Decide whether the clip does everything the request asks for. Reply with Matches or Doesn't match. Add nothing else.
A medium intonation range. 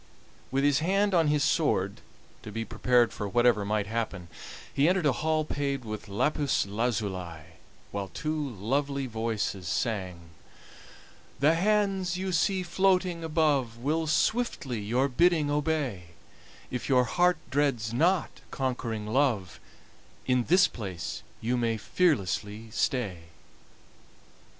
Doesn't match